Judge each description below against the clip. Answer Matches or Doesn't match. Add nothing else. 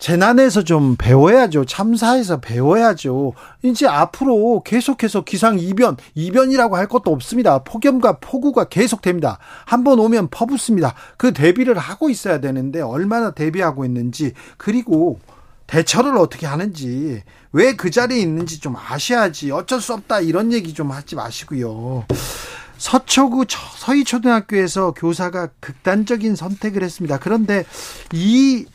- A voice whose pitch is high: Matches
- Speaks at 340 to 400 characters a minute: Doesn't match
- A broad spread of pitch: Matches